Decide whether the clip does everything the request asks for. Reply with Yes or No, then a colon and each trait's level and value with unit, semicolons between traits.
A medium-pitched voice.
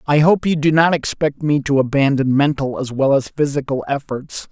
Yes: medium, 145 Hz